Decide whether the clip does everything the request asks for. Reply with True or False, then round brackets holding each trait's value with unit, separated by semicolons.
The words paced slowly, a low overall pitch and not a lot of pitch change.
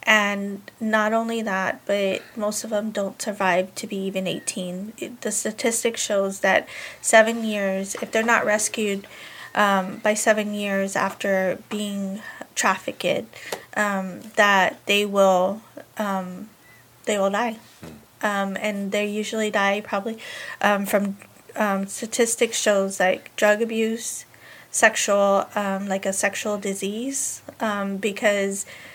False (130 wpm; 205 Hz; 1.9 semitones)